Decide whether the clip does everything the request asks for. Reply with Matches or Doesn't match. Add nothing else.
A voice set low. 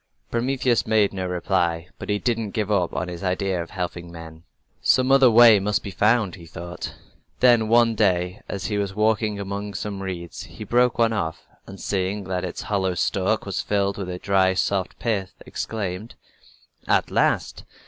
Matches